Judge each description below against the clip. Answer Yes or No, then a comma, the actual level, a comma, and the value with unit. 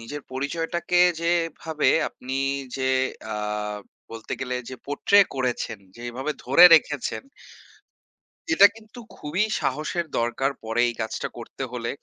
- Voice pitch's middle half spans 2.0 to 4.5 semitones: No, wide, 5.4 semitones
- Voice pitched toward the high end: No, low, 135 Hz